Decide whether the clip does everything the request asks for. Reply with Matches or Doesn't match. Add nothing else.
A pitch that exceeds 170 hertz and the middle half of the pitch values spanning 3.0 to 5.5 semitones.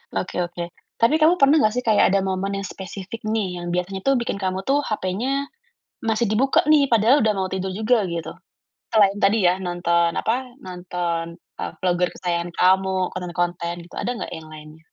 Matches